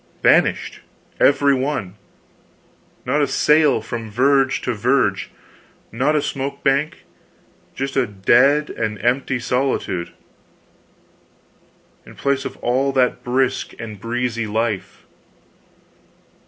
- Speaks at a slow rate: Yes, slow, 105 wpm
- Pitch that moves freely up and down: No, average, 3.2 semitones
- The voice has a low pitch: Yes, low, 130 Hz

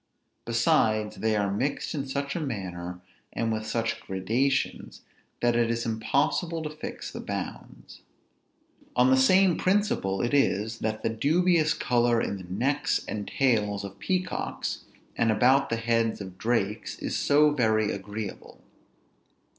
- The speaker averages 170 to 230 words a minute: No, average, 145 wpm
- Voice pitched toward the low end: Yes, low, 115 Hz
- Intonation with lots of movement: No, average, 4.6 semitones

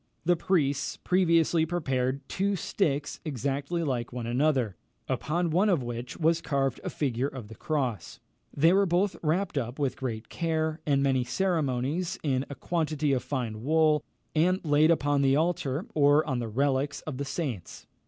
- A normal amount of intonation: Yes, average, 4.0 semitones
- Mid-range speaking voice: Yes, medium, 145 Hz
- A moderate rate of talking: Yes, average, 165 wpm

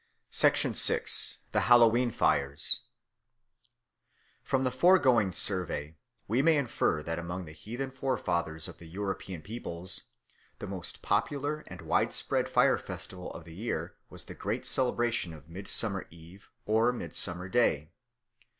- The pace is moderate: No, slow, 130 wpm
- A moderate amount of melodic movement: No, wide, 6.3 semitones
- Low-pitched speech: Yes, very low, 95 Hz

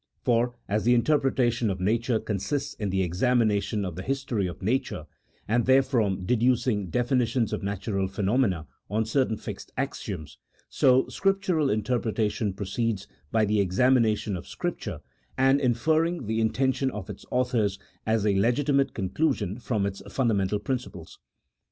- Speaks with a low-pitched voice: Yes, low, 115 Hz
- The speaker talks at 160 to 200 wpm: No, average, 145 wpm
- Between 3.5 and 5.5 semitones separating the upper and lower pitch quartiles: Yes, average, 4.2 semitones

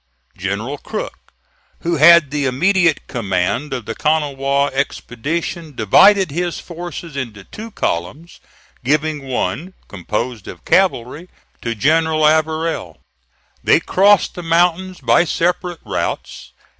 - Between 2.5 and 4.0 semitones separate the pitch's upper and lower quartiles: No, wide, 5.5 semitones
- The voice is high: No, medium, 150 Hz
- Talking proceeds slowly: Yes, slow, 115 wpm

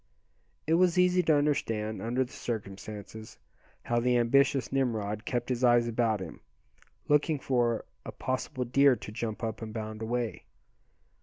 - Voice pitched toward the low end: Yes, low, 120 Hz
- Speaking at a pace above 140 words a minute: Yes, average, 150 wpm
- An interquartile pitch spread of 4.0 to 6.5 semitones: No, average, 3.6 semitones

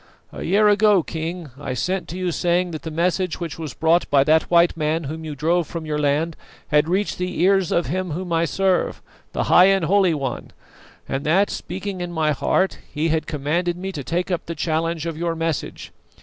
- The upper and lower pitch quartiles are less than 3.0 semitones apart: Yes, narrow, 2.6 semitones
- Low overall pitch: No, medium, 170 Hz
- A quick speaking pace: Yes, fast, 210 wpm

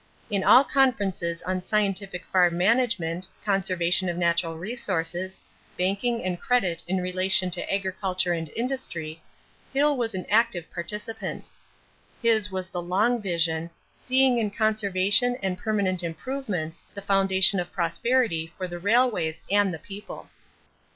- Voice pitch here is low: No, high, 190 Hz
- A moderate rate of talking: No, slow, 130 wpm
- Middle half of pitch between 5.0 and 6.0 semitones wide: No, average, 3.8 semitones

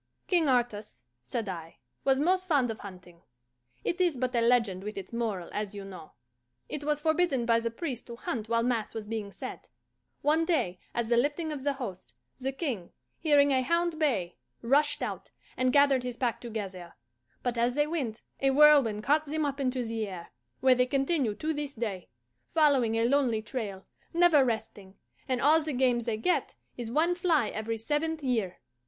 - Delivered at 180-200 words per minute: Yes, average, 185 wpm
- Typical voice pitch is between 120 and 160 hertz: No, very high, 250 Hz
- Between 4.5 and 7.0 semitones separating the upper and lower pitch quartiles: Yes, average, 5.1 semitones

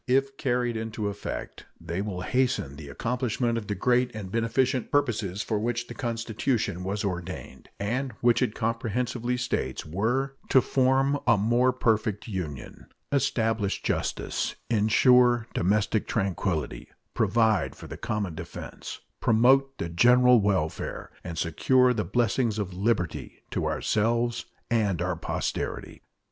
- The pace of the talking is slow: Yes, slow, 130 wpm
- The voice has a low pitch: Yes, low, 115 Hz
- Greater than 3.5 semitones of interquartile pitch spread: Yes, average, 4.0 semitones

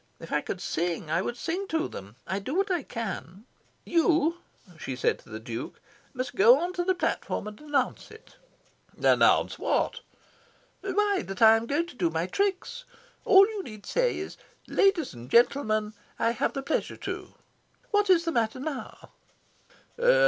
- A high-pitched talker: Yes, very high, 270 Hz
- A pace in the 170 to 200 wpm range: Yes, average, 175 wpm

